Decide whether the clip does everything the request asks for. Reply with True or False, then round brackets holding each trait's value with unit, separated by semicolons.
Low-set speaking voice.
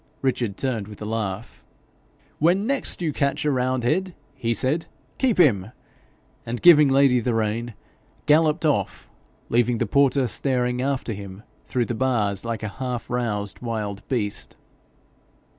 True (125 Hz)